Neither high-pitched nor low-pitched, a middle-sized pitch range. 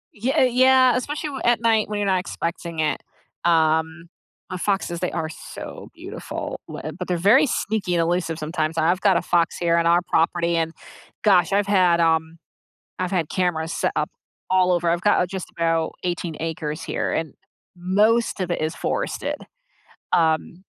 Yes: medium, 175 Hz; average, 3.3 semitones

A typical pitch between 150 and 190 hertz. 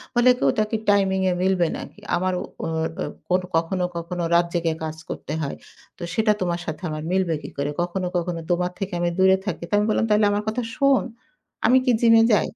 Yes: medium, 185 Hz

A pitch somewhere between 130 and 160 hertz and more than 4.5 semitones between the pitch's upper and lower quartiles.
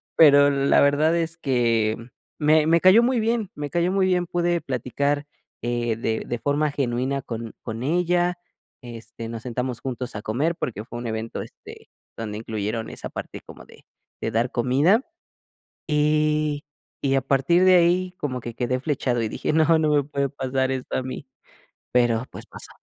Yes: low, 135 Hz; average, 5.0 semitones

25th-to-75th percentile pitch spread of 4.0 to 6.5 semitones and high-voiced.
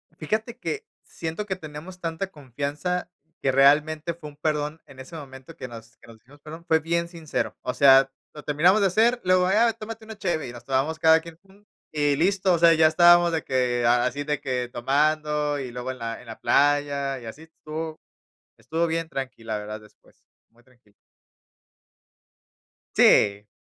No: average, 4.4 semitones; medium, 150 Hz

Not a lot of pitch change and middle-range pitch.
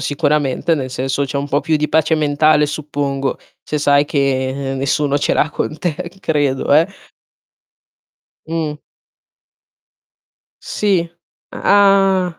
Yes: narrow, 2.3 semitones; medium, 150 Hz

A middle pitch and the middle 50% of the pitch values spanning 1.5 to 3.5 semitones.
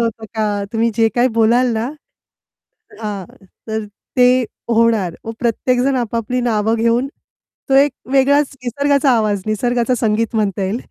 No: high, 230 Hz; narrow, 2.5 semitones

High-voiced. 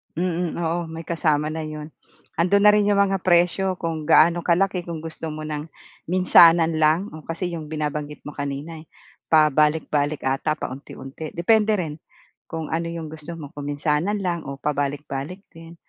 No: medium, 160 Hz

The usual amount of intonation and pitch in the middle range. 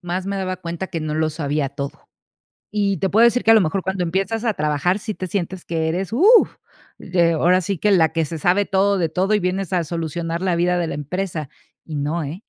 Yes: average, 3.2 semitones; medium, 180 Hz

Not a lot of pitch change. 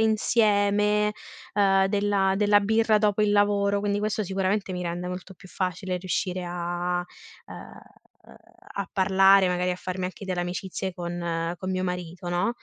Yes: narrow, 2.3 semitones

